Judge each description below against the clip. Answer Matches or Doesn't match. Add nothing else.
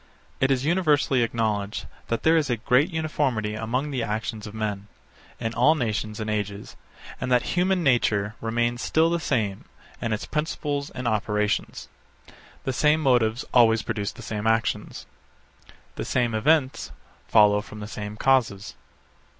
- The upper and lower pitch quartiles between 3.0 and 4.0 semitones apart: Doesn't match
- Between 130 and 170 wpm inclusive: Matches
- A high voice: Doesn't match